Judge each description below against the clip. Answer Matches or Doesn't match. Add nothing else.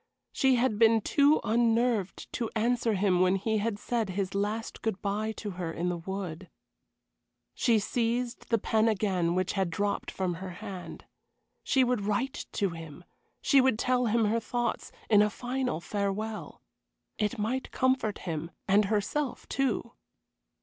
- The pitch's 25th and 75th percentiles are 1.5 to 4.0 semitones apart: Matches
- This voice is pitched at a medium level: Doesn't match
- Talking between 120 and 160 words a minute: Matches